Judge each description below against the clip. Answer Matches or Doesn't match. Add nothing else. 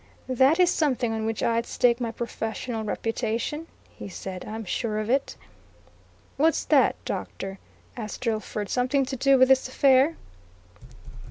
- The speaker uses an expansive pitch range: Doesn't match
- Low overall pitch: Doesn't match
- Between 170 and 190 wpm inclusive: Doesn't match